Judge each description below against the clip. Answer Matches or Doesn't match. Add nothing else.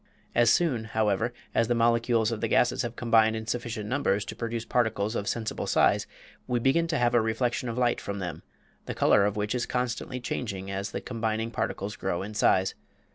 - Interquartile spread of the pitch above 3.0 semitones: Doesn't match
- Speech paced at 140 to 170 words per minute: Doesn't match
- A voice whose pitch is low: Matches